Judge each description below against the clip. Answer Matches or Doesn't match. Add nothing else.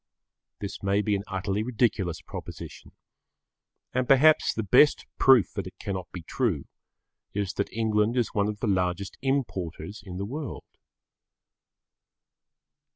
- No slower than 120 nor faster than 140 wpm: Matches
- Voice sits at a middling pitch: Doesn't match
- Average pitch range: Matches